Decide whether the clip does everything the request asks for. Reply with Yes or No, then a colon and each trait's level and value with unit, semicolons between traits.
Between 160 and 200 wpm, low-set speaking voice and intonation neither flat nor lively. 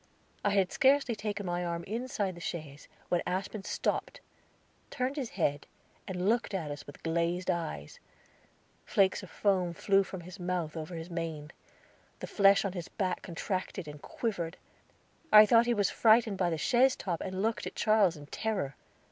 No: average, 175 wpm; medium, 185 Hz; average, 3.9 semitones